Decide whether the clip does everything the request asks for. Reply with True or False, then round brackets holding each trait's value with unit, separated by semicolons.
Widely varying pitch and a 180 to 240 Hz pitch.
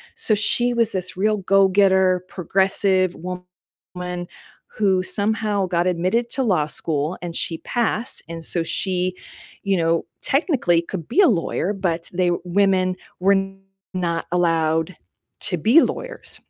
False (2.6 semitones; 185 Hz)